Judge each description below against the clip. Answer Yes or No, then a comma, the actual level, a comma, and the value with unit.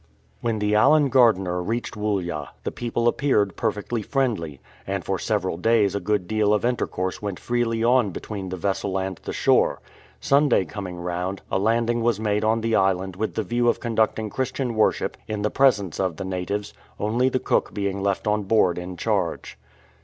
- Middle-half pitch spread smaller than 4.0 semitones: Yes, average, 3.5 semitones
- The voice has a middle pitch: No, low, 105 Hz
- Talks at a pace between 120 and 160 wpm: No, average, 185 wpm